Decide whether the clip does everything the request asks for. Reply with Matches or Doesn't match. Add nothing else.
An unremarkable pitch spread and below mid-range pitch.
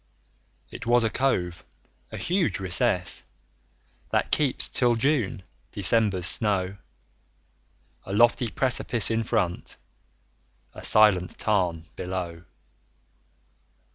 Matches